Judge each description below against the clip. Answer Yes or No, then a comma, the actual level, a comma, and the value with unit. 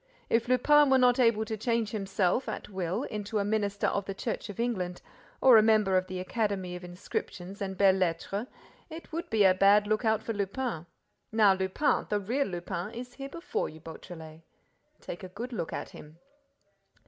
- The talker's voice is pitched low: No, high, 205 Hz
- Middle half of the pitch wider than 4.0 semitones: No, average, 3.7 semitones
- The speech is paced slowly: No, average, 185 wpm